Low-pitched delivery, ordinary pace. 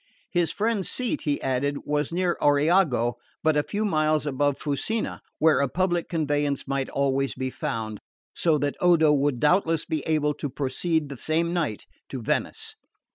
No: medium, 150 Hz; average, 165 wpm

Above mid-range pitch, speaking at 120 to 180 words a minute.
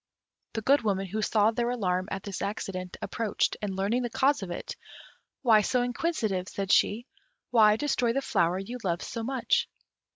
Yes: high, 215 Hz; average, 175 wpm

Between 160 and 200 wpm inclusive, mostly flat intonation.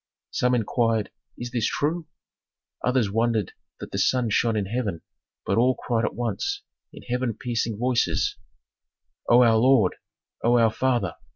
No: average, 150 wpm; narrow, 2.1 semitones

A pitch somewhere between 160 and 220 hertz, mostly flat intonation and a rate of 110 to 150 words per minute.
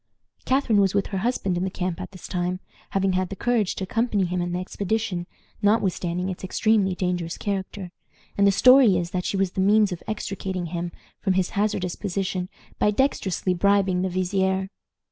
No: high, 190 Hz; narrow, 2.0 semitones; average, 185 wpm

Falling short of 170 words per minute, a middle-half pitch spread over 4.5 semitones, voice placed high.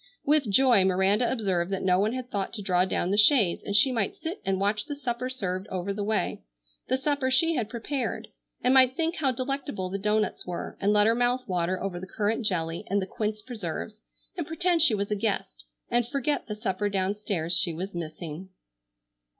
No: average, 200 wpm; average, 5.2 semitones; high, 210 Hz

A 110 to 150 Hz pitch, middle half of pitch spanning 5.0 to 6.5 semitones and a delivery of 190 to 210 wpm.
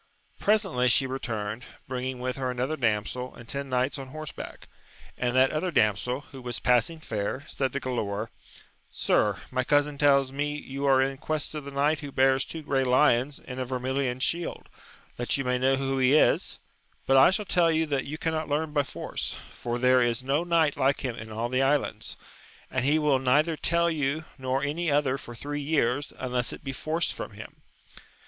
No: low, 135 Hz; average, 2.7 semitones; average, 195 wpm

